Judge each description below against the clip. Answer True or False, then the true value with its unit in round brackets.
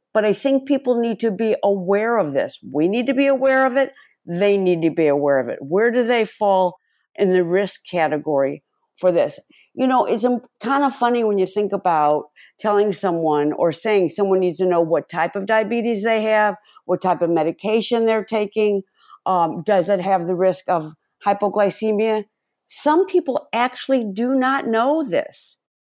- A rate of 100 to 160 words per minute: False (185 wpm)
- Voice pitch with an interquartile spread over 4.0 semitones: True (4.7 semitones)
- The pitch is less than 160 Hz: False (210 Hz)